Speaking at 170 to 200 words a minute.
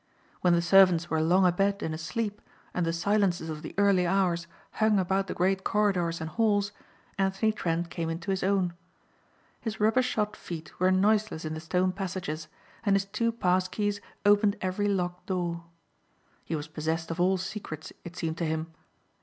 Yes: average, 175 wpm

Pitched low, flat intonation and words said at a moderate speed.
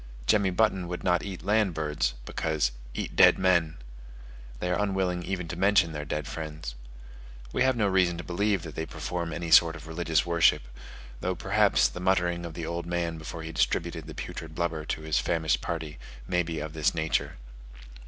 Yes: very low, 85 Hz; narrow, 2.1 semitones; average, 190 wpm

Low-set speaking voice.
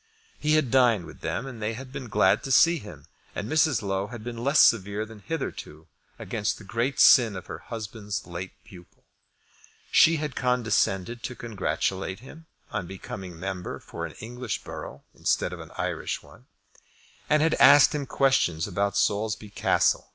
Yes: low, 110 Hz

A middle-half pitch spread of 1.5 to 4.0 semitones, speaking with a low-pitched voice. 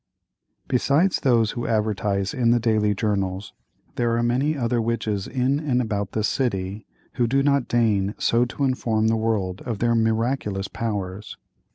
Yes: average, 3.0 semitones; low, 115 Hz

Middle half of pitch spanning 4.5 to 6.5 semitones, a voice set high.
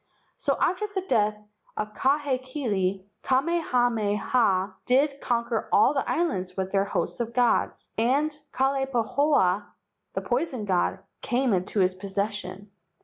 Yes: average, 5.3 semitones; high, 240 Hz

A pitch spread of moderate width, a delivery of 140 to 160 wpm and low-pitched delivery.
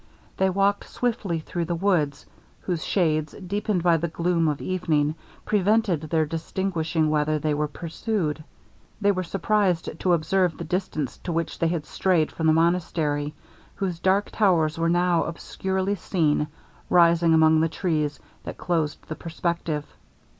No: average, 3.0 semitones; average, 150 wpm; medium, 170 Hz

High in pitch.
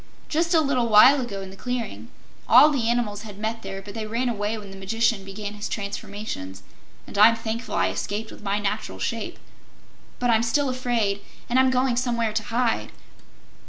Yes: high, 225 Hz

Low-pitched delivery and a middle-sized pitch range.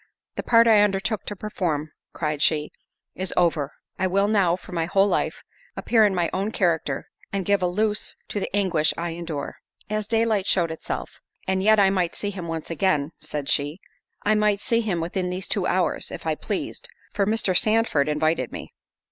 No: medium, 185 Hz; average, 4.0 semitones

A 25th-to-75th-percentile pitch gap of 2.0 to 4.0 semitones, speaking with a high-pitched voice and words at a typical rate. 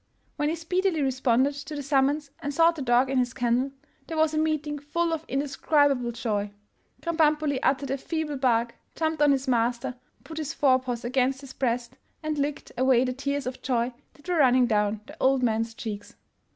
Yes: average, 3.2 semitones; very high, 270 Hz; average, 190 wpm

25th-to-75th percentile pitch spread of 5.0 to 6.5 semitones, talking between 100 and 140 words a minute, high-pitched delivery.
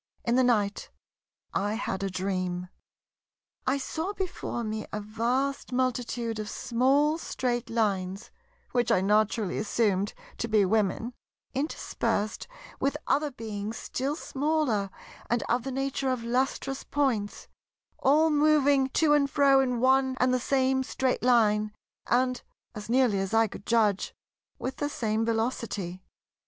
No: average, 4.1 semitones; slow, 135 wpm; high, 240 Hz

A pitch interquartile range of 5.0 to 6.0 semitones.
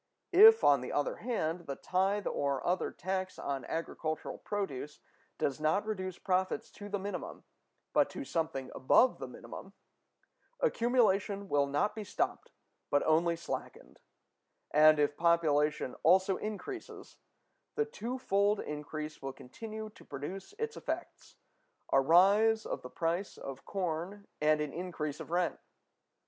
Yes: average, 5.3 semitones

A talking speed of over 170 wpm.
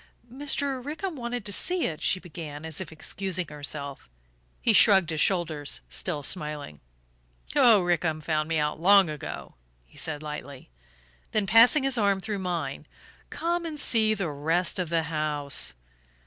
No: average, 155 wpm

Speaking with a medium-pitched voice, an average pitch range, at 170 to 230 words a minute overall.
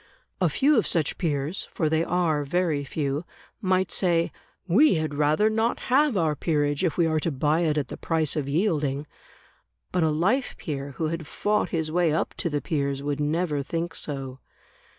Yes: medium, 160 Hz; average, 3.3 semitones; average, 190 wpm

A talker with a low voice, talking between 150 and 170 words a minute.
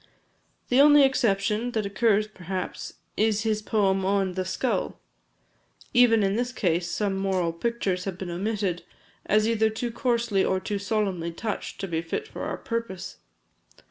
No: high, 205 Hz; average, 155 wpm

